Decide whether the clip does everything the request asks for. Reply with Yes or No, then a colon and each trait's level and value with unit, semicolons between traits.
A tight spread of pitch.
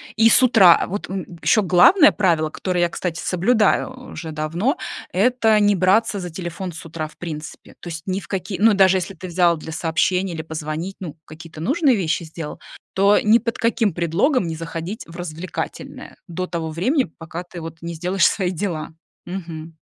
No: average, 3.7 semitones